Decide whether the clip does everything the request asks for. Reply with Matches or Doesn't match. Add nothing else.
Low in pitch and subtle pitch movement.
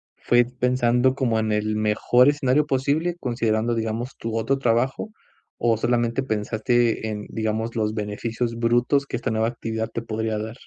Matches